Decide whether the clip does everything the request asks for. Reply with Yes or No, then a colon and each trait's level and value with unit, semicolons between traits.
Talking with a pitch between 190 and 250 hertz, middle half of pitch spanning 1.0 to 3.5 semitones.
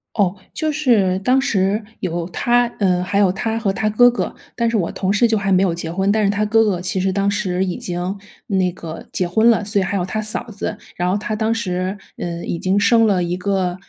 Yes: high, 195 Hz; average, 2.9 semitones